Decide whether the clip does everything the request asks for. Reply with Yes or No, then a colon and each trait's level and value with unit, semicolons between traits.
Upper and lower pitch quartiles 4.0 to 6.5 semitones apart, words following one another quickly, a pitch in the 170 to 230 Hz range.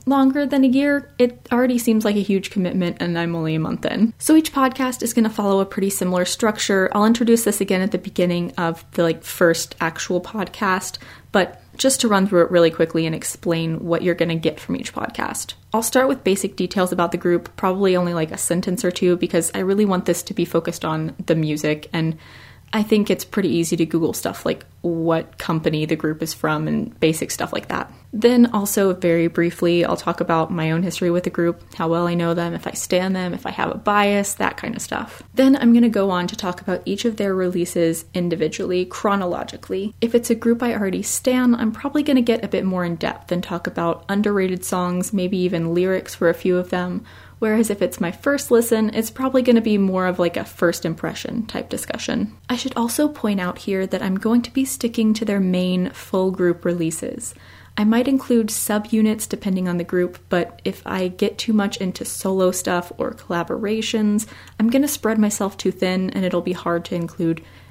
Yes: average, 4.3 semitones; fast, 220 wpm; medium, 185 Hz